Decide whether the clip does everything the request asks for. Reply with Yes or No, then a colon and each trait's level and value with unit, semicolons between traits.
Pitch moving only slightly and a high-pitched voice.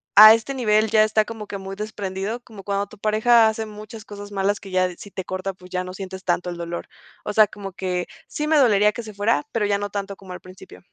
Yes: narrow, 2.3 semitones; high, 205 Hz